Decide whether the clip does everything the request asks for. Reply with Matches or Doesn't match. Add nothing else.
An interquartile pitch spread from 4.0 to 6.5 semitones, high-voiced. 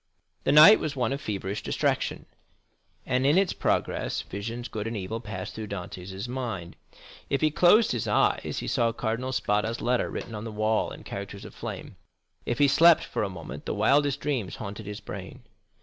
Doesn't match